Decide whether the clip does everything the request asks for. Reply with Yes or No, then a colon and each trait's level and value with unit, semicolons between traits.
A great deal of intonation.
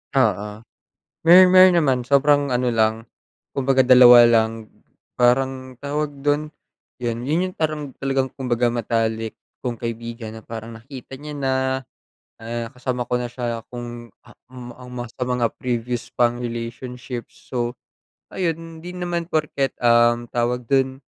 No: average, 2.7 semitones